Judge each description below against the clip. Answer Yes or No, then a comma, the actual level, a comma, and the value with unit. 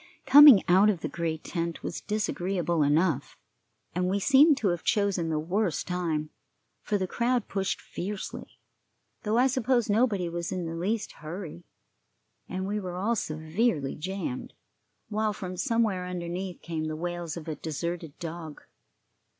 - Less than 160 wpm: Yes, average, 150 wpm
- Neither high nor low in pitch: Yes, medium, 180 Hz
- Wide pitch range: No, average, 3.9 semitones